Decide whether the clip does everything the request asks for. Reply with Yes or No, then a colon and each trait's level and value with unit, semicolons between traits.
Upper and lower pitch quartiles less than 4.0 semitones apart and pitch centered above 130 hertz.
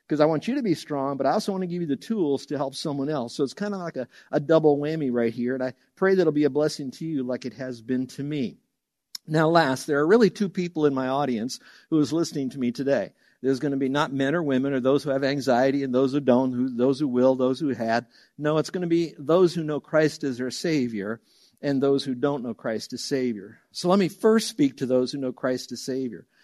Yes: average, 3.3 semitones; medium, 140 Hz